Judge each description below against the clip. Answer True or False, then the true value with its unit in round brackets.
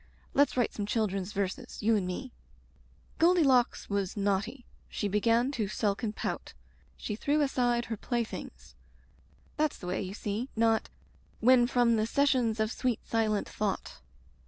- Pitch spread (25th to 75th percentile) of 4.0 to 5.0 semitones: False (3.4 semitones)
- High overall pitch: True (225 Hz)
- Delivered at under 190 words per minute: True (160 wpm)